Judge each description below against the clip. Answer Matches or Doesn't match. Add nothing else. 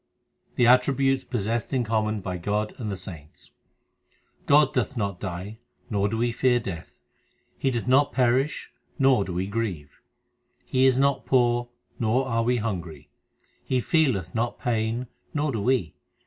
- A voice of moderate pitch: Doesn't match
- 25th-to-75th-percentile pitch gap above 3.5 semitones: Matches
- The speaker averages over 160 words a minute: Doesn't match